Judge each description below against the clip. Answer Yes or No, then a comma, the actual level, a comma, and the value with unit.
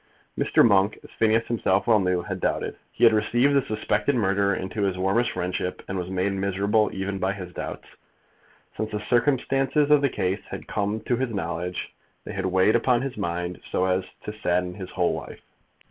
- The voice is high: No, low, 100 Hz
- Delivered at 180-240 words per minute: Yes, average, 190 wpm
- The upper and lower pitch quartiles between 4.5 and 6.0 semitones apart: No, average, 3.7 semitones